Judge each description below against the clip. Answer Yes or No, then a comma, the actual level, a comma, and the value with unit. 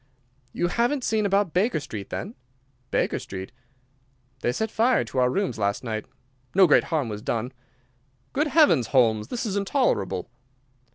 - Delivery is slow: No, average, 155 wpm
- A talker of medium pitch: Yes, medium, 170 Hz